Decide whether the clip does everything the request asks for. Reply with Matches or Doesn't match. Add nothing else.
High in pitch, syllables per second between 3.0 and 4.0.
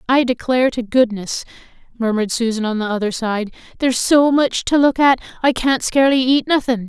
Doesn't match